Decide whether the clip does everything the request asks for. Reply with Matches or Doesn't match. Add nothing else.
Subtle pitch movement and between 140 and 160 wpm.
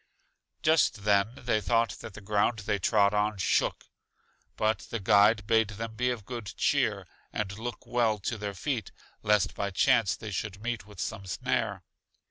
Doesn't match